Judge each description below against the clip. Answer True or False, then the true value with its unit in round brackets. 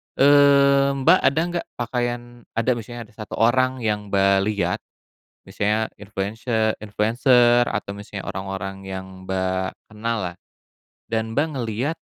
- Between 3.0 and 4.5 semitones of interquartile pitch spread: True (3.8 semitones)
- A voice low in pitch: True (110 Hz)